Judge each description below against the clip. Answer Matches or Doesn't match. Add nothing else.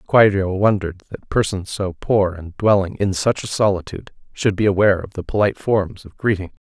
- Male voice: Matches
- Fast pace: Doesn't match